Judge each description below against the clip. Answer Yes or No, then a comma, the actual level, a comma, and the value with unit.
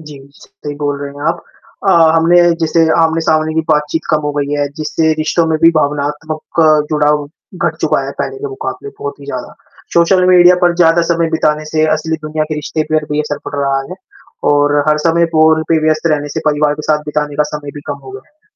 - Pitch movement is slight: Yes, narrow, 1.8 semitones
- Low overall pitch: No, medium, 155 Hz